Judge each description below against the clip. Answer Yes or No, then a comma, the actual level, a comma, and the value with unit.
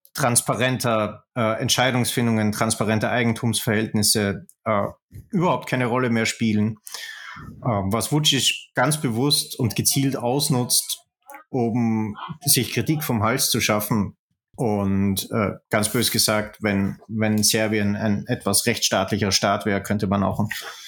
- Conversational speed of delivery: No, slow, 120 wpm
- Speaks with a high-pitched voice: No, low, 115 Hz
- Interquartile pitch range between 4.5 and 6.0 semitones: No, average, 3.1 semitones